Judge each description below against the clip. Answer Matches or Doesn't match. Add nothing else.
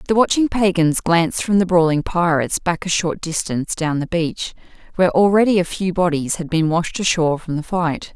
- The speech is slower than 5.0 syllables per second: Doesn't match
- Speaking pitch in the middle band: Matches